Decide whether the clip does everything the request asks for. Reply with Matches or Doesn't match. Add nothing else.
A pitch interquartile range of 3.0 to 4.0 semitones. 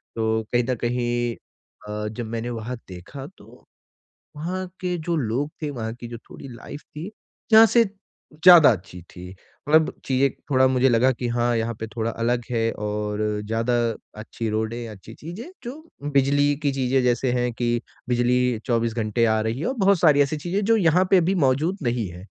Doesn't match